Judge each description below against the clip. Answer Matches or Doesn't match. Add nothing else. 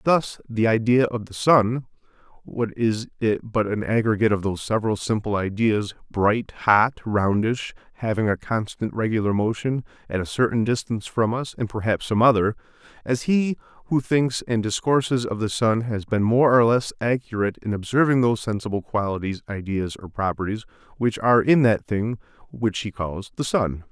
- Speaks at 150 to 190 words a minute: Matches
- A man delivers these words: Matches